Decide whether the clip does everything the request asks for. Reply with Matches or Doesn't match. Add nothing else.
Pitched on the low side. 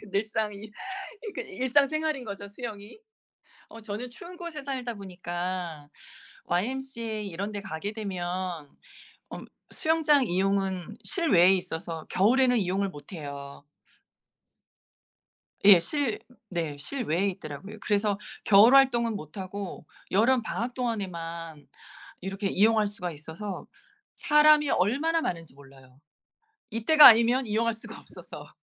Doesn't match